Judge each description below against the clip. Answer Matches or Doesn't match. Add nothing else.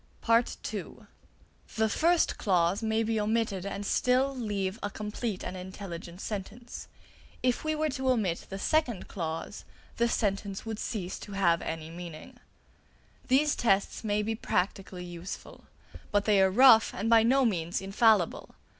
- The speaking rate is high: Doesn't match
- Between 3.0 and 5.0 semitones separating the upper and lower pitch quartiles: Matches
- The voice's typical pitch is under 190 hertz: Doesn't match